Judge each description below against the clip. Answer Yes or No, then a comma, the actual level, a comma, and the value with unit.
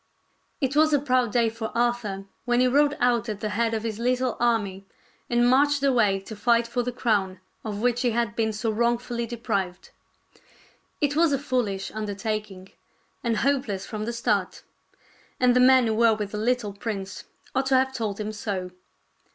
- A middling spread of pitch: Yes, average, 3.0 semitones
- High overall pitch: Yes, high, 235 Hz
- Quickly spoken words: No, average, 190 wpm